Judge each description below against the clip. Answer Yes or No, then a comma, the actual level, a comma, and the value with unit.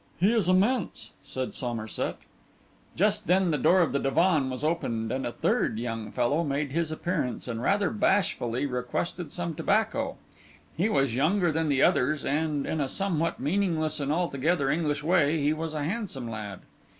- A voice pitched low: No, medium, 155 Hz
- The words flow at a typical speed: Yes, average, 170 wpm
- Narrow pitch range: No, average, 5.1 semitones